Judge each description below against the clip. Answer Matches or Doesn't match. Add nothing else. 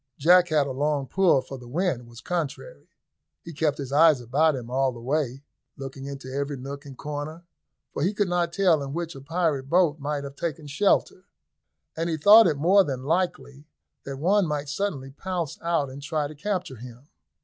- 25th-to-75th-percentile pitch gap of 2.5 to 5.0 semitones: Matches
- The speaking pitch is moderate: Matches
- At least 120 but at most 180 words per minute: Doesn't match